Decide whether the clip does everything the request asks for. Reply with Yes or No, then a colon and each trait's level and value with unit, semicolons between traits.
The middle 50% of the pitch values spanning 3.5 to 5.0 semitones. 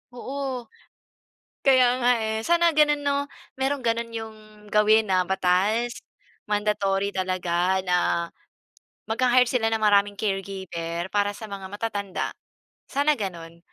Yes: average, 4.4 semitones